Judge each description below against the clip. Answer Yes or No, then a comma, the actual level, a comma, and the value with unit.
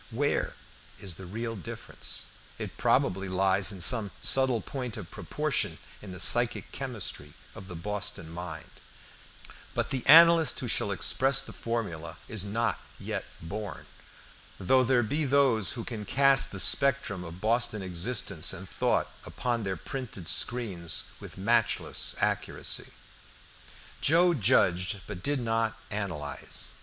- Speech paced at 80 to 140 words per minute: Yes, slow, 135 wpm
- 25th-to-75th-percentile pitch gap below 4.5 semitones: No, average, 5.1 semitones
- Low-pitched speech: Yes, low, 105 Hz